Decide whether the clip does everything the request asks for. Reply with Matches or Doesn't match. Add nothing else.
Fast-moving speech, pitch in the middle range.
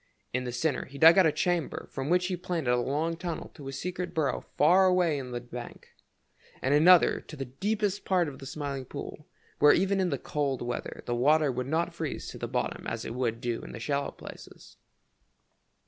Matches